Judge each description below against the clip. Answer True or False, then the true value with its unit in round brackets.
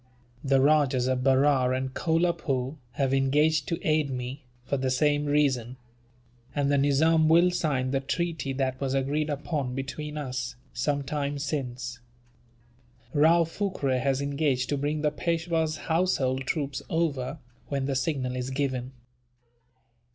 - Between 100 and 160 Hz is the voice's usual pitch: True (140 Hz)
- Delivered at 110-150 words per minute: True (140 wpm)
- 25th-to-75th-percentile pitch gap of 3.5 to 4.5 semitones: False (2.7 semitones)